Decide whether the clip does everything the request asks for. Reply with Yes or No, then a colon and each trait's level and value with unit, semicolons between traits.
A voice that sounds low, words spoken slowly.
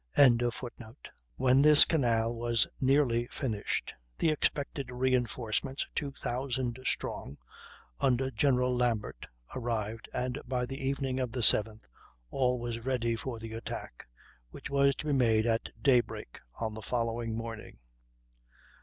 Yes: low, 125 Hz; slow, 130 wpm